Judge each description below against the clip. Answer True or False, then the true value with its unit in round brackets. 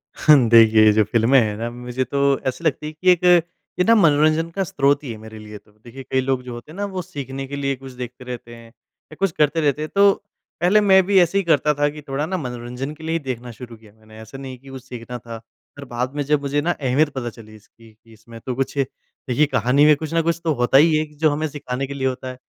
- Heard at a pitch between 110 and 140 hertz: True (135 Hz)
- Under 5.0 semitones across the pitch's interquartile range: True (4.2 semitones)